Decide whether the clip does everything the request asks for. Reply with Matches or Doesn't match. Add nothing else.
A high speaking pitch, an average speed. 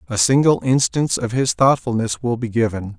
Doesn't match